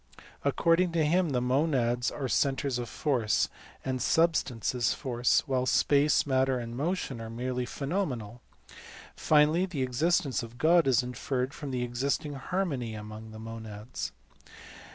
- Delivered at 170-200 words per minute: No, average, 145 wpm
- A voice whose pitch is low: Yes, low, 130 Hz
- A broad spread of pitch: No, average, 3.7 semitones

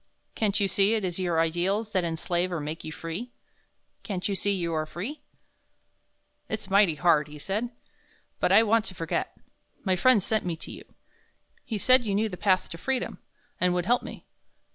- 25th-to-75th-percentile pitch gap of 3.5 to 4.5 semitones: Yes, average, 4.2 semitones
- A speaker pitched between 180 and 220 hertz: Yes, high, 190 Hz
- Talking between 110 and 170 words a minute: No, average, 190 wpm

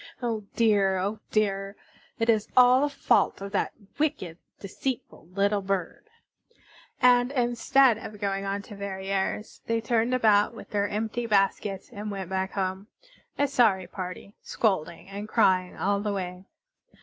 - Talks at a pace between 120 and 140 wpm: No, average, 150 wpm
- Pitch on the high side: Yes, high, 205 Hz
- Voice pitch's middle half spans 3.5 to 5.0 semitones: No, average, 2.9 semitones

